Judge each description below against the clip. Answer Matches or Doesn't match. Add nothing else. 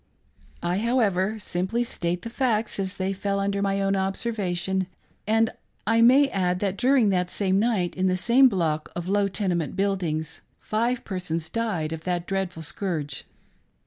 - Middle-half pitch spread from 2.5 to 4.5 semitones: Matches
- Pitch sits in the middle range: Doesn't match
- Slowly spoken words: Doesn't match